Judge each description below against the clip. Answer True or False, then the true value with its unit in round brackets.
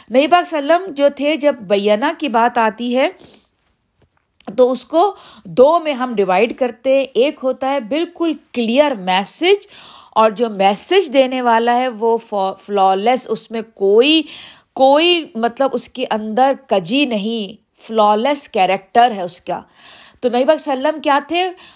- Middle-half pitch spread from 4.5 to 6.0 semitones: True (4.9 semitones)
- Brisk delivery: False (150 wpm)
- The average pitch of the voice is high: True (255 Hz)